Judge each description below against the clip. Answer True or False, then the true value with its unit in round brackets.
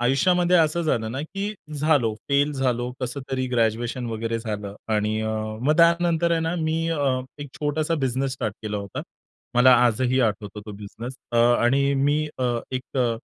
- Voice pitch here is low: True (130 Hz)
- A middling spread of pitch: True (5.0 semitones)